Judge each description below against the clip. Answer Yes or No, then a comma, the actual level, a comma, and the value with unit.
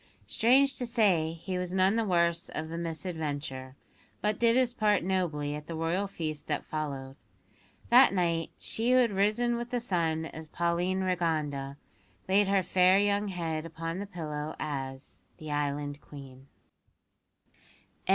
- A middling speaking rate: Yes, average, 150 wpm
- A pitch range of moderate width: Yes, average, 4.7 semitones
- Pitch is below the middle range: No, medium, 170 Hz